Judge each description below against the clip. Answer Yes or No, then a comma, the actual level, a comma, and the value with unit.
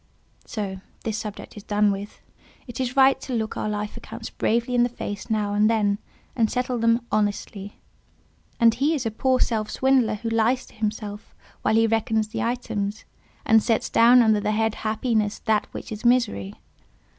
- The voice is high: Yes, high, 220 Hz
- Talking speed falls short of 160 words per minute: No, average, 180 wpm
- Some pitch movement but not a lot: No, narrow, 2.3 semitones